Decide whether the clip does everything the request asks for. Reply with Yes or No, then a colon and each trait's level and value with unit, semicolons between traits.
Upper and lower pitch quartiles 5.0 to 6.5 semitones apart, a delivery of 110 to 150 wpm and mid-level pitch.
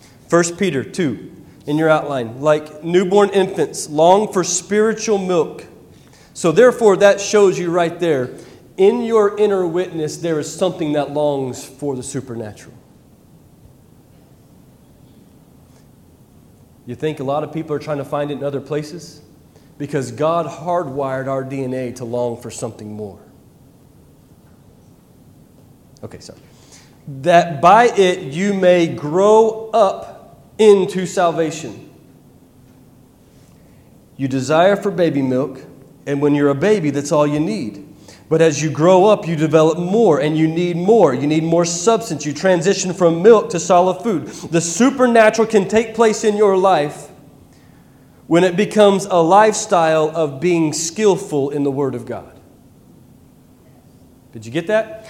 Yes: average, 5.3 semitones; average, 140 wpm; medium, 165 Hz